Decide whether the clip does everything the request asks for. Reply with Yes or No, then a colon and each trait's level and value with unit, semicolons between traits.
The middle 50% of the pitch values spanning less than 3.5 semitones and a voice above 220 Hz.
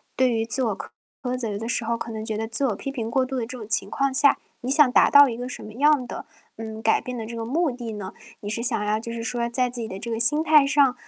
Yes: average, 2.8 semitones; high, 235 Hz